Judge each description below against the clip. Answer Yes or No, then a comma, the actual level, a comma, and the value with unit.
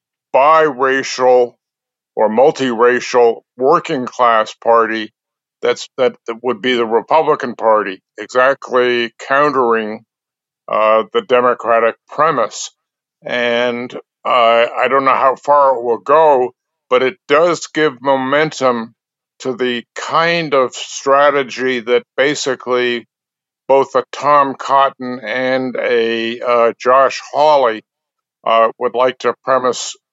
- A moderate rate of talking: No, slow, 110 wpm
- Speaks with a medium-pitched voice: No, low, 125 Hz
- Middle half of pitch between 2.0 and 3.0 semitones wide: Yes, narrow, 2.4 semitones